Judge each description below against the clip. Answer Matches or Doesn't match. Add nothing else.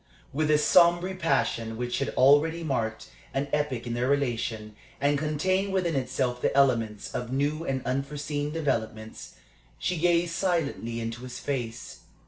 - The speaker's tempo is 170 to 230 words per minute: Doesn't match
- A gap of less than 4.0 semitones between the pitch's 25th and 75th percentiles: Doesn't match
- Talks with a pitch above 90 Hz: Matches